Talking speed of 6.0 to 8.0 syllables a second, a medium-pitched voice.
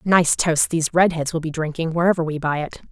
Yes: 6.2 syllables/s; medium, 165 Hz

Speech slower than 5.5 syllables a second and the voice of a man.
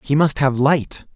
Yes: 4.0 syllables/s; male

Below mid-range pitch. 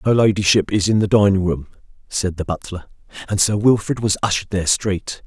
Yes: low, 100 Hz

